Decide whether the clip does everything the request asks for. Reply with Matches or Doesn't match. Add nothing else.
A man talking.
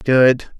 Matches